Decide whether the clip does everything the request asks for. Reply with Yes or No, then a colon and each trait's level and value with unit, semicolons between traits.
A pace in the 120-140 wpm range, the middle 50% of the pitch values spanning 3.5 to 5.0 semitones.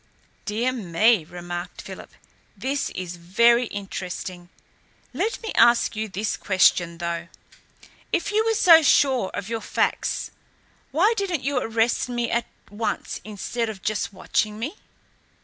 No: slow, 135 wpm; wide, 5.6 semitones